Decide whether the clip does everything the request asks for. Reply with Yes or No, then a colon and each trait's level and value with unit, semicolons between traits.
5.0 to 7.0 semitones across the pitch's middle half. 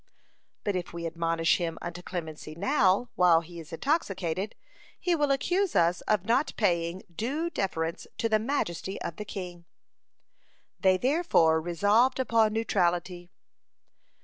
Yes: average, 5.3 semitones